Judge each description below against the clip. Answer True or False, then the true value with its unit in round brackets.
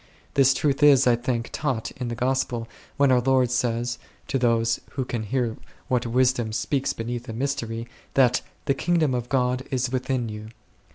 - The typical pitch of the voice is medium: False (125 Hz)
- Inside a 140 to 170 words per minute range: False (180 wpm)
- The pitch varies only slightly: True (2.2 semitones)